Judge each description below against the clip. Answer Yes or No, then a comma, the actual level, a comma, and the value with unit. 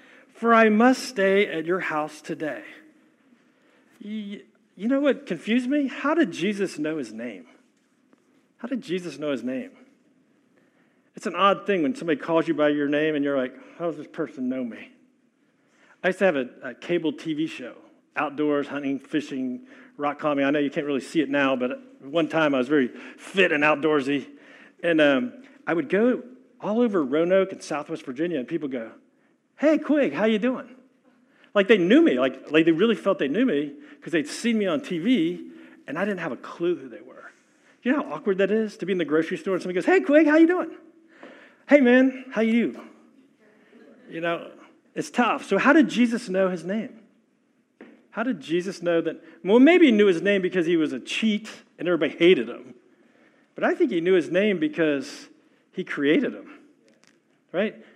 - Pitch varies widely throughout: Yes, wide, 8.5 semitones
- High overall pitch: Yes, high, 235 Hz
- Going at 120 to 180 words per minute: No, average, 195 wpm